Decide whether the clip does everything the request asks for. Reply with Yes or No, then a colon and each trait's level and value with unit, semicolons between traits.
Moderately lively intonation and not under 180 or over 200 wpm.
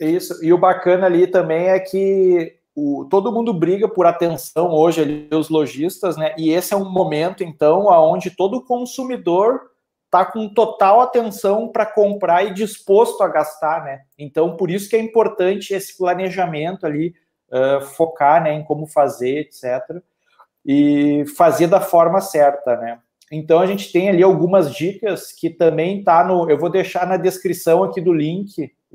No: average, 3.6 semitones; average, 165 wpm